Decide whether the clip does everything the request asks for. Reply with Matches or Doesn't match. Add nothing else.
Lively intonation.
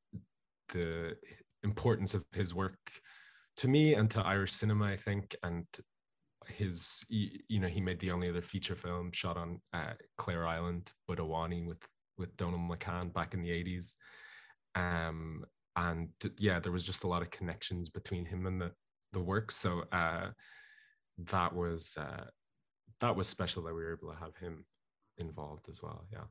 Doesn't match